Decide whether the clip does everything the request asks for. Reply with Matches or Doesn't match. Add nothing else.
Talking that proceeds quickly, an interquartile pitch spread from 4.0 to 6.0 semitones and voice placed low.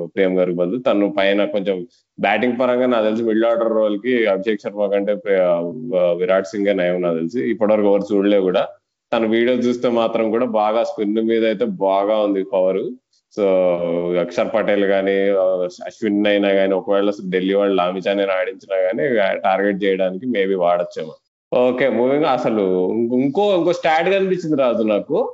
Doesn't match